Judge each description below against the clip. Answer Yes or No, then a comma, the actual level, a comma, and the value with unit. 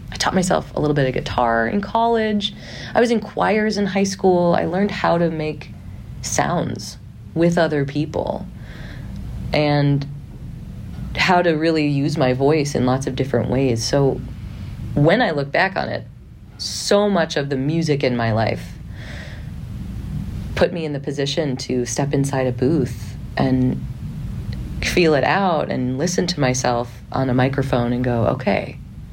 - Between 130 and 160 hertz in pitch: Yes, medium, 140 Hz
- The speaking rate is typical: Yes, average, 160 wpm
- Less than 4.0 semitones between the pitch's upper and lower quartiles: No, average, 5.2 semitones